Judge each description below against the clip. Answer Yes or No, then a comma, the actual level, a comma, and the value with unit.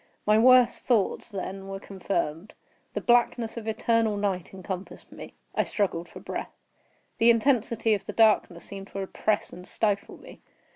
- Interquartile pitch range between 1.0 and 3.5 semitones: Yes, average, 2.9 semitones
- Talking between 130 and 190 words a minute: Yes, average, 155 wpm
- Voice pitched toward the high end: Yes, high, 210 Hz